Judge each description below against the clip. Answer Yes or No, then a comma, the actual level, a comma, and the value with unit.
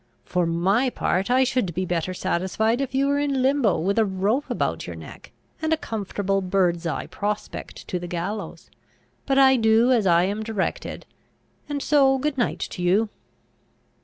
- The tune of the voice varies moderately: No, wide, 6.1 semitones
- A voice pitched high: Yes, high, 215 Hz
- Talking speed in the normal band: Yes, average, 175 wpm